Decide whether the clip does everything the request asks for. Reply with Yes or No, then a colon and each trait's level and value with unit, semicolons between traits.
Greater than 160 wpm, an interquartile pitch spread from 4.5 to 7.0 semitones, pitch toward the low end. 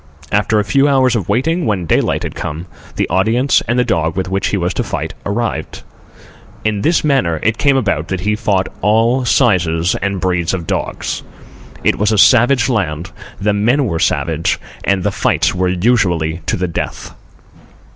Yes: average, 180 wpm; average, 5.1 semitones; low, 100 Hz